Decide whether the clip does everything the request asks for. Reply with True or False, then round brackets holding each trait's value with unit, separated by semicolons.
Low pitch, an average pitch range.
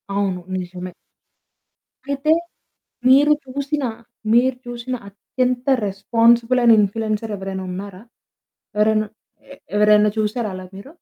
False (220 Hz; 4.1 semitones)